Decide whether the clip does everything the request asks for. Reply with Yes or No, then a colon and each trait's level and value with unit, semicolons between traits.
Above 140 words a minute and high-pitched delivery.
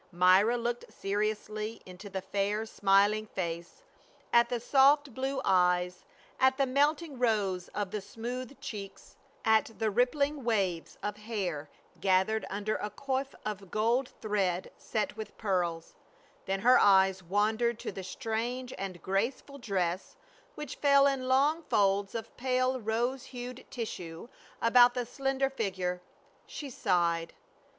No: slow, 135 wpm; high, 215 Hz